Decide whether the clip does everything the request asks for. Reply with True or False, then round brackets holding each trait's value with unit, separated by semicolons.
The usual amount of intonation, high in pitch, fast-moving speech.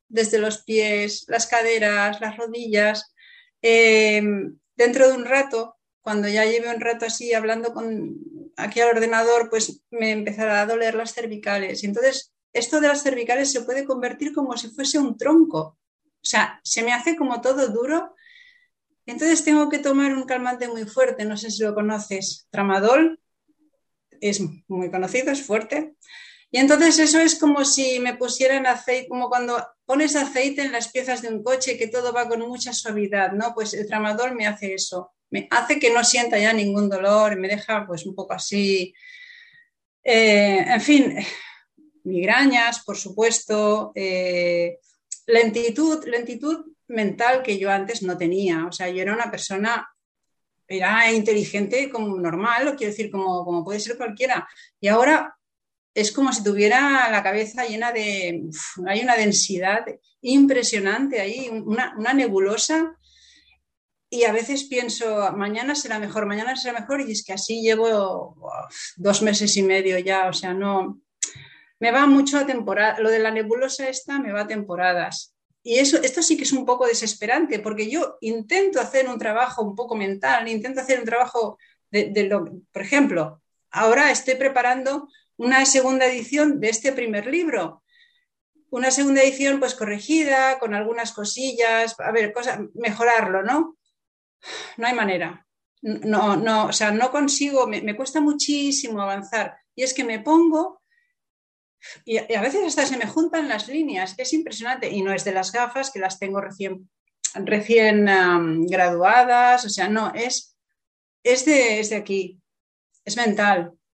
False (4.2 semitones; 230 Hz; 165 wpm)